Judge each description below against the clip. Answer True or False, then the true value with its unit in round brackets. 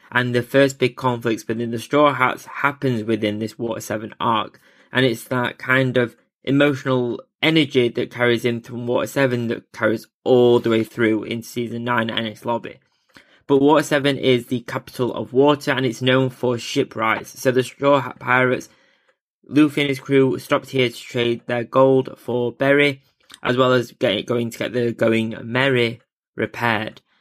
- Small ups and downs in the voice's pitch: True (2.3 semitones)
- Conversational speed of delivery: True (180 wpm)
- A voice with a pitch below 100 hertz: False (125 Hz)